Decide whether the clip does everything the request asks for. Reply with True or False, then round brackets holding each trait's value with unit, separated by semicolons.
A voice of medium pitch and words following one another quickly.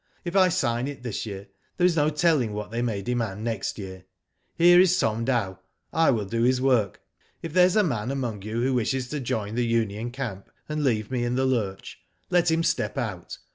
False (120 Hz; 215 wpm)